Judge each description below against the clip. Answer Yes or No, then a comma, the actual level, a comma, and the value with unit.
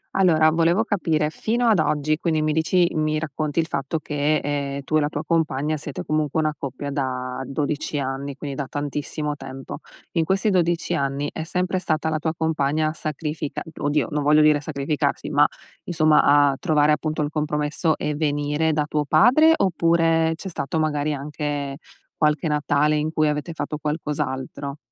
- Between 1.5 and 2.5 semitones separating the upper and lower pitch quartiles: Yes, narrow, 1.8 semitones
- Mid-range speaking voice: Yes, medium, 150 Hz